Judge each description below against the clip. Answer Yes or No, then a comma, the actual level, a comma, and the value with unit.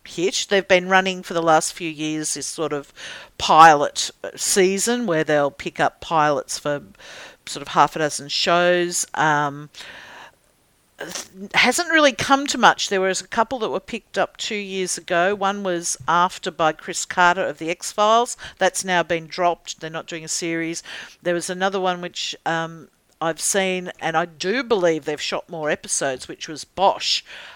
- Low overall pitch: No, medium, 175 Hz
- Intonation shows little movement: No, average, 3.4 semitones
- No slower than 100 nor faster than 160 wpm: No, average, 175 wpm